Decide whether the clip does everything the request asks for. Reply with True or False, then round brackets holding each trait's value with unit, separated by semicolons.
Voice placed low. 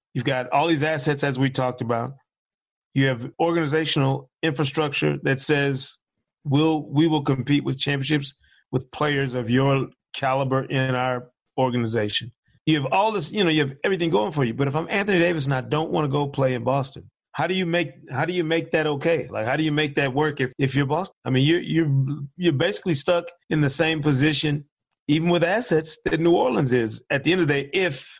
False (145 Hz)